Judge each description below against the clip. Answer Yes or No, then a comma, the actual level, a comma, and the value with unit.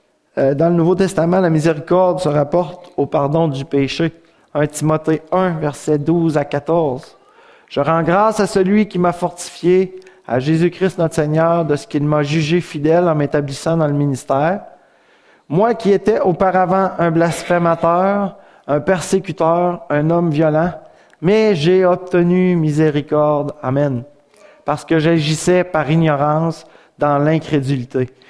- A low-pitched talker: No, medium, 165 Hz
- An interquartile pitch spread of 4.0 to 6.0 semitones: No, average, 3.3 semitones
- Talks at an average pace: No, slow, 140 wpm